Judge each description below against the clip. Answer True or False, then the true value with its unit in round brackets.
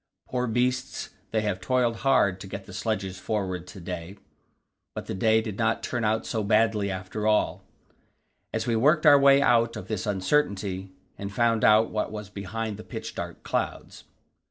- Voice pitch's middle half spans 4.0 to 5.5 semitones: False (3.0 semitones)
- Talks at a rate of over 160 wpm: True (180 wpm)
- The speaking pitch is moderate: False (110 Hz)